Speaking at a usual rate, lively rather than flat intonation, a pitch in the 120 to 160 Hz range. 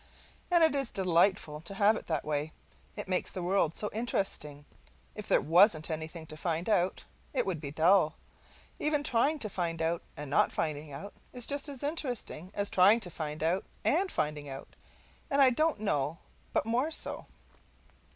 No: average, 180 wpm; wide, 6.9 semitones; medium, 185 Hz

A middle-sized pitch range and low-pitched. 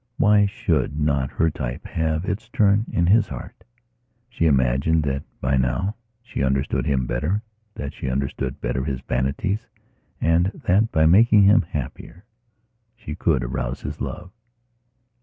No: wide, 6.6 semitones; very low, 80 Hz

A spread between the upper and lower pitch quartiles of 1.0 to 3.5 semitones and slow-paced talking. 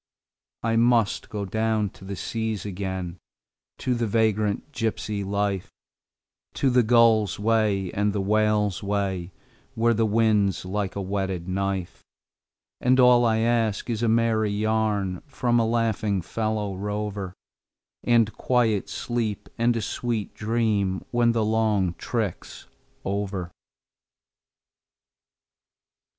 Yes: narrow, 2.4 semitones; slow, 120 wpm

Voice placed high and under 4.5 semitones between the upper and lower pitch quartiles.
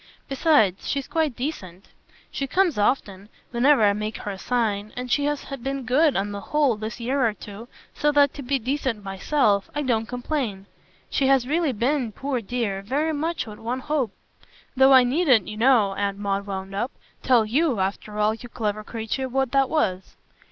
No: high, 245 Hz; average, 4.9 semitones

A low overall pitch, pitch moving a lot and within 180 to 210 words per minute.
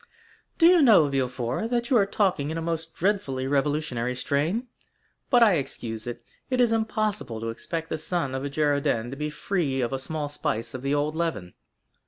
No: medium, 150 Hz; wide, 6.5 semitones; average, 195 wpm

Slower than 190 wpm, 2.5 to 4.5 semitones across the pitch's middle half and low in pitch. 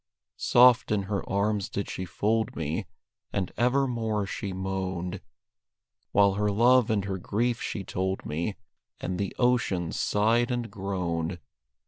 Yes: slow, 135 wpm; average, 3.2 semitones; low, 100 Hz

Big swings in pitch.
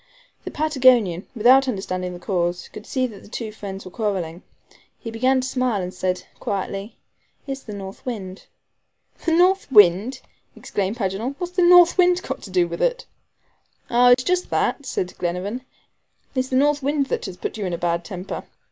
Yes: wide, 6.1 semitones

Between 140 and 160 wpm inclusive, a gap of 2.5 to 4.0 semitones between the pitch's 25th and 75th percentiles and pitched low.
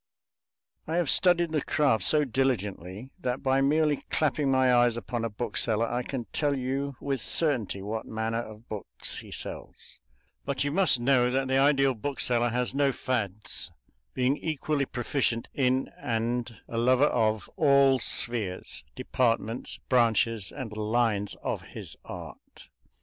Yes: average, 145 wpm; average, 3.3 semitones; low, 125 Hz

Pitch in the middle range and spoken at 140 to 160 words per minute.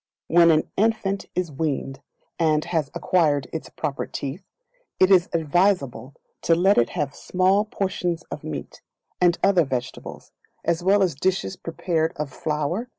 Yes: medium, 165 Hz; average, 155 wpm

